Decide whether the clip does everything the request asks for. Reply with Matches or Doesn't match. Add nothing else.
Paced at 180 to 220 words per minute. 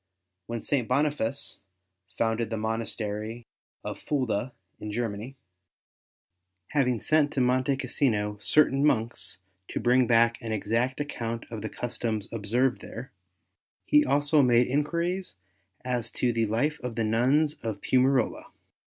Doesn't match